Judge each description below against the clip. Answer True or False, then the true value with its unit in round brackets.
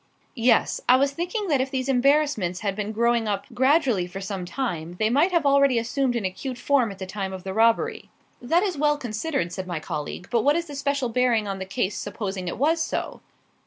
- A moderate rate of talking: False (220 wpm)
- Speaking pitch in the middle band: False (240 Hz)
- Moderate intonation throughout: False (6.2 semitones)